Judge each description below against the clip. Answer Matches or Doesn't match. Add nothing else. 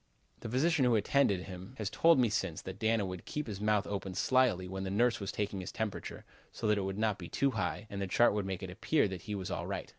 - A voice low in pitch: Matches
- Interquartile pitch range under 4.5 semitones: Matches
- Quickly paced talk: Matches